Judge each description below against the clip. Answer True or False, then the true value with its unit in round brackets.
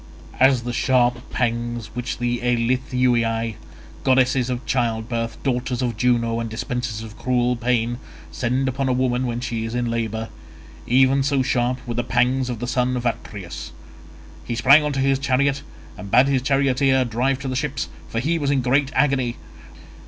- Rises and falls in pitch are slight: True (1.9 semitones)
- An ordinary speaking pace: True (170 wpm)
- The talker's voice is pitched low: True (125 Hz)